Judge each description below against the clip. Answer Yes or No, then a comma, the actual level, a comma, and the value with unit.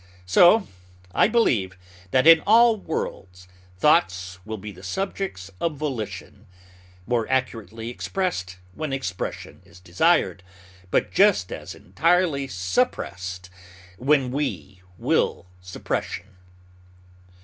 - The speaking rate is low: Yes, slow, 105 wpm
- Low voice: Yes, low, 115 Hz